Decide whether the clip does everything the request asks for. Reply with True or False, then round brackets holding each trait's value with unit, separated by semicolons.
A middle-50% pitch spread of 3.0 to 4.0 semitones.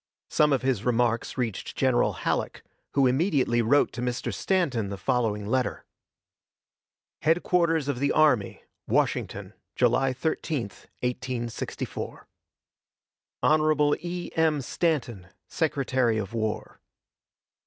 False (4.5 semitones)